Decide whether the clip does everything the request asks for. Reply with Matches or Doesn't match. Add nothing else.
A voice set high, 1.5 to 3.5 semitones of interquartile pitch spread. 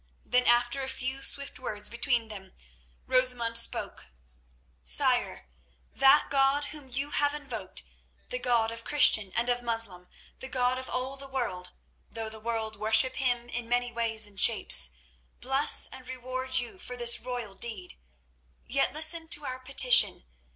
Matches